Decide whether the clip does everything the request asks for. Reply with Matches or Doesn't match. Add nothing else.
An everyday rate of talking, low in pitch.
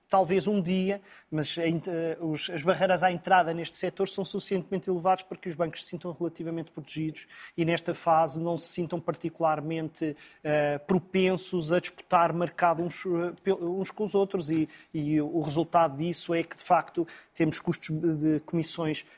Doesn't match